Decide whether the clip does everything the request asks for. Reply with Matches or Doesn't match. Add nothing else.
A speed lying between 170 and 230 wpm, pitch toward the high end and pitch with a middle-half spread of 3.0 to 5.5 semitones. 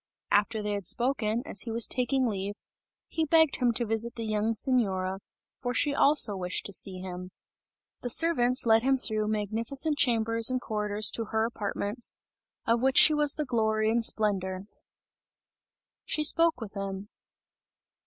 Doesn't match